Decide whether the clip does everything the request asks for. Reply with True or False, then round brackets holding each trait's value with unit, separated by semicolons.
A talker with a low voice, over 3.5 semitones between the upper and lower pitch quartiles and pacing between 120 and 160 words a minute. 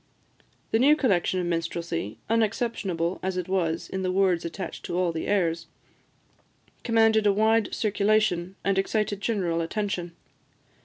False (190 Hz; 3.9 semitones; 140 wpm)